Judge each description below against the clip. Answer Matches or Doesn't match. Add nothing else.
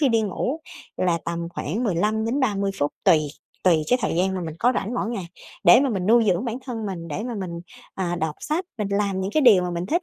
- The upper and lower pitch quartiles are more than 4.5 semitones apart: Matches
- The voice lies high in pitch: Matches